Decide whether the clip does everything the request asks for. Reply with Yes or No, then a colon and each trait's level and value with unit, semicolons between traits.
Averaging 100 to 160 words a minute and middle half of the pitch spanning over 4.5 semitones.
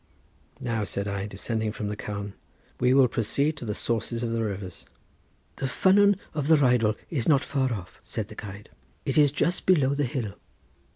No: average, 185 wpm; average, 5.0 semitones